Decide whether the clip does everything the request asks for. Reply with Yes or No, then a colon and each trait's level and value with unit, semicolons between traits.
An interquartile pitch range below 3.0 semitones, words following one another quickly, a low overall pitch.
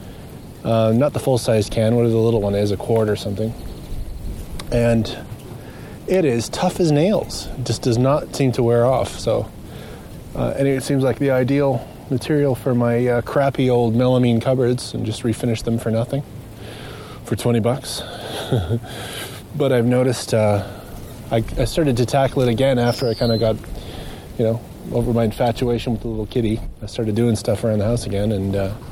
No: narrow, 2.5 semitones; average, 185 wpm; low, 120 Hz